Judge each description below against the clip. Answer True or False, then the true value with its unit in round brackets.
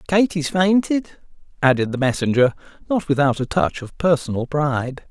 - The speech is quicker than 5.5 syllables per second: False (5.2 syllables/s)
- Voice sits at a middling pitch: True (150 Hz)